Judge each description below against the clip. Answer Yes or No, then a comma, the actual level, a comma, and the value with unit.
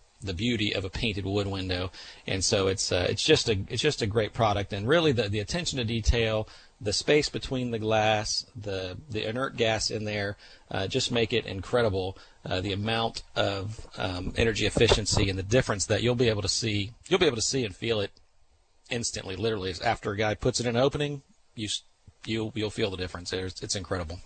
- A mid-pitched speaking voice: No, low, 105 Hz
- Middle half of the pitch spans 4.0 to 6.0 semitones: No, average, 3.3 semitones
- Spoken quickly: Yes, fast, 210 wpm